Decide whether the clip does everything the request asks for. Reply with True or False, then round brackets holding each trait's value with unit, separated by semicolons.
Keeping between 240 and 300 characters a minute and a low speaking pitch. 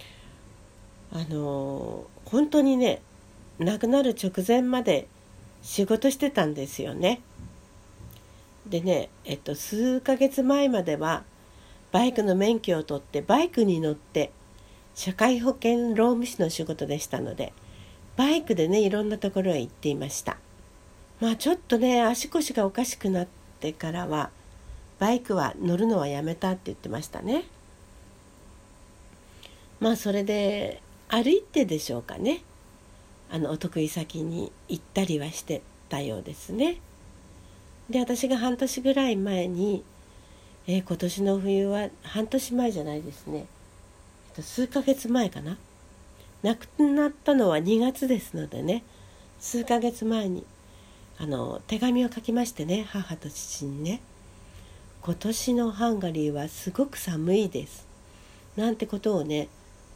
False (255 characters per minute; 185 Hz)